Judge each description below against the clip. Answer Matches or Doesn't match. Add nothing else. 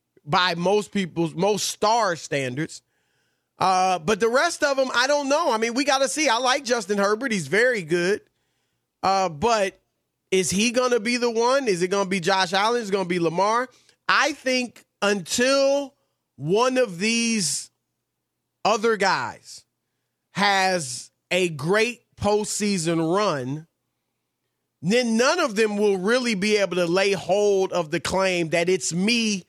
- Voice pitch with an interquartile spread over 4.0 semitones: Matches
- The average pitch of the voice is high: Matches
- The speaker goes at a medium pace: Matches